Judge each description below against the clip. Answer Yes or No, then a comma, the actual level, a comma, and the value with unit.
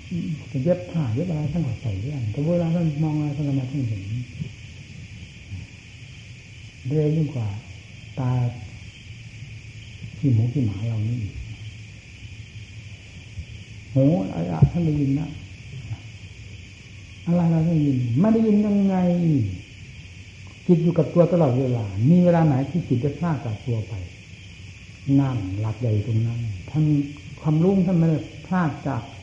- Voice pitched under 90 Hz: No, low, 120 Hz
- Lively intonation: Yes, wide, 6.1 semitones